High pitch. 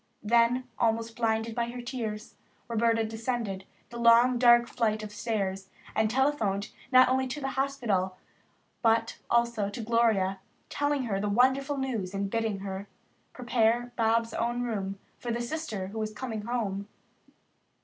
Yes: high, 230 Hz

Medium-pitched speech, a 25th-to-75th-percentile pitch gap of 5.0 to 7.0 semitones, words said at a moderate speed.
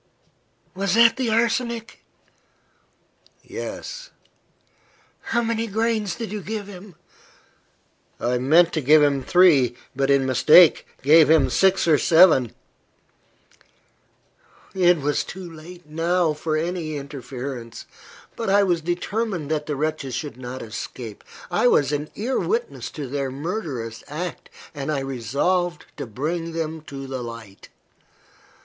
No: medium, 160 Hz; wide, 5.5 semitones; slow, 130 wpm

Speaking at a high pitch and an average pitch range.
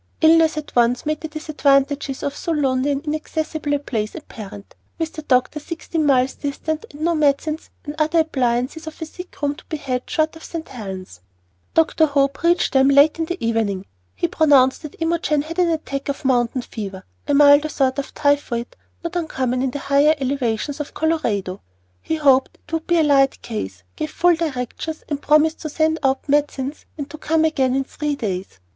Yes: very high, 285 Hz; average, 3.4 semitones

